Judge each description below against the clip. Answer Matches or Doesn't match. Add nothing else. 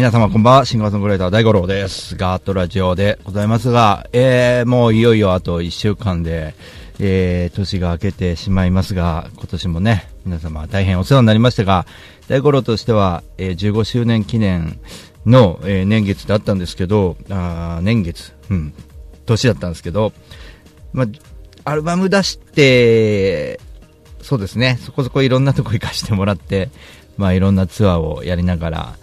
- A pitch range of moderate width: Matches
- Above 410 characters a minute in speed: Doesn't match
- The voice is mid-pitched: Doesn't match